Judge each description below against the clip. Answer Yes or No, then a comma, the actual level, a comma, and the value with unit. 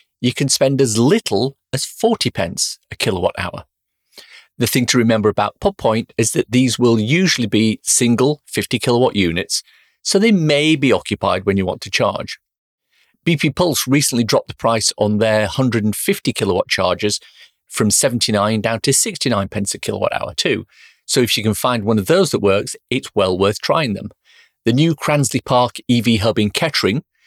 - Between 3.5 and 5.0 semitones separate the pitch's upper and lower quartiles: Yes, average, 4.2 semitones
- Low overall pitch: Yes, low, 120 Hz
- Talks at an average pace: Yes, average, 180 wpm